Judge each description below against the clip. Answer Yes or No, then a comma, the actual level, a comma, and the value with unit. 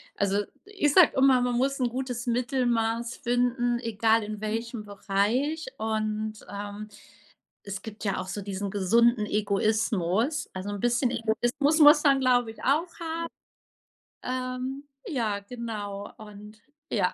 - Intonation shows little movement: No, average, 3.5 semitones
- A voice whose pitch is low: No, high, 230 Hz